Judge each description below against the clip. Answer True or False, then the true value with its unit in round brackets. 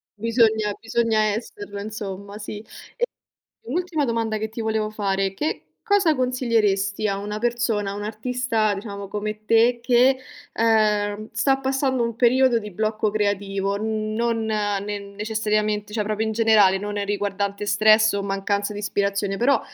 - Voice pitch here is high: True (215 Hz)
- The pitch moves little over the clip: True (2.0 semitones)